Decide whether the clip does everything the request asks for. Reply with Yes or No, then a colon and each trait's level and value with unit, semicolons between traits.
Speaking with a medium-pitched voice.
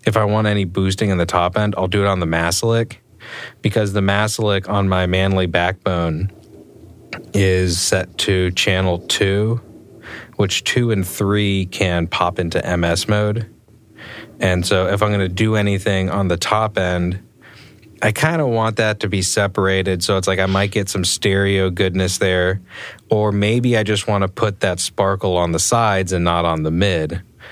No: low, 100 Hz